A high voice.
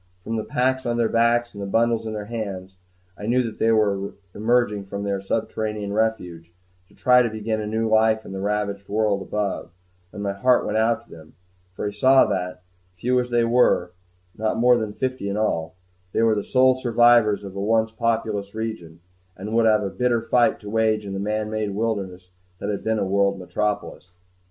No: low, 110 Hz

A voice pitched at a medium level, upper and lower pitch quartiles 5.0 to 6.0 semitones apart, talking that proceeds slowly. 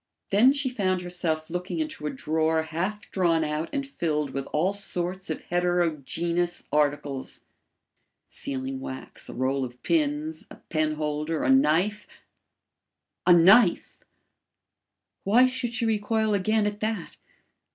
Yes: medium, 175 Hz; wide, 5.4 semitones; slow, 130 wpm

